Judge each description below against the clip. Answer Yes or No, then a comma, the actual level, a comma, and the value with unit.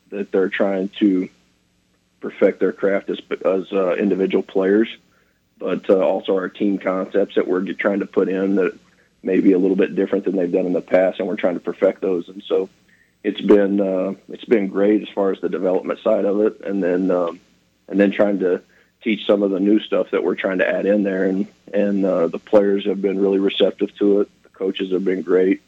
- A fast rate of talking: Yes, fast, 220 wpm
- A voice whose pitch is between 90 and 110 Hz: Yes, very low, 95 Hz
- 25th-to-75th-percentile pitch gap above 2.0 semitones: No, narrow, 1.3 semitones